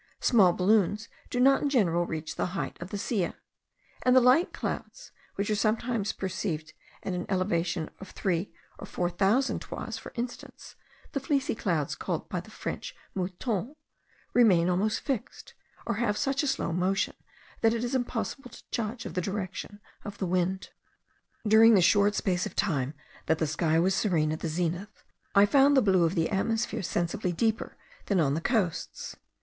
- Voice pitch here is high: Yes, high, 195 Hz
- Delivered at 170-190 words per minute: Yes, average, 175 wpm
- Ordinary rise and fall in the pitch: Yes, average, 4.6 semitones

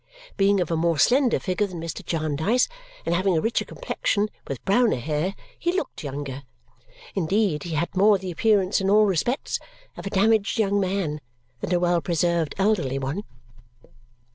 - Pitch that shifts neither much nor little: Yes, average, 4.4 semitones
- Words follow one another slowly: No, average, 165 wpm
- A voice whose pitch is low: No, medium, 185 Hz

